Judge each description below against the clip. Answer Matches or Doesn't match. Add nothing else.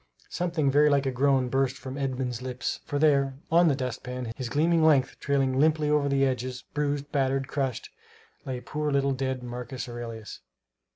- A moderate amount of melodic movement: Doesn't match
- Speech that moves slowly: Doesn't match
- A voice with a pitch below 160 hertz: Matches